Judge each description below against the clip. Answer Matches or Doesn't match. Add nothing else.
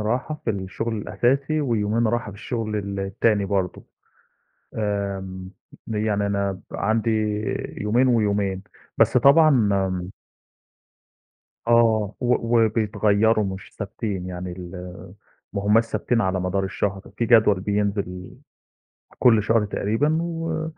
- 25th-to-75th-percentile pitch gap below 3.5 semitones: Matches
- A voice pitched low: Matches